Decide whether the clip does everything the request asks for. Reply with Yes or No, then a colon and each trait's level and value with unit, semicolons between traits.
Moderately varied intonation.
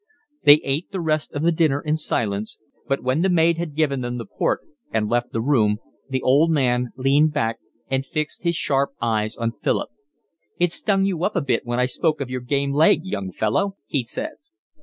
Yes: average, 4.6 semitones